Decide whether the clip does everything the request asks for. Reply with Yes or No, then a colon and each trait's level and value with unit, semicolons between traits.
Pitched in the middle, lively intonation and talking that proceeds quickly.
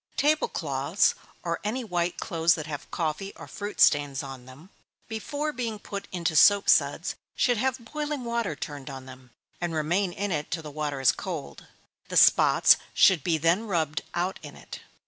No: medium, 175 Hz; wide, 6.3 semitones; average, 185 wpm